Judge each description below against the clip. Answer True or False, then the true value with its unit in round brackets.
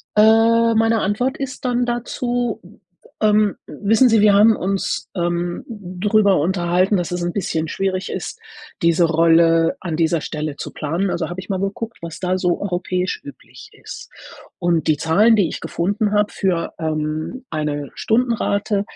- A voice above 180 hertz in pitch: True (190 Hz)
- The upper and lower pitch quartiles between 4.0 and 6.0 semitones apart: True (4.5 semitones)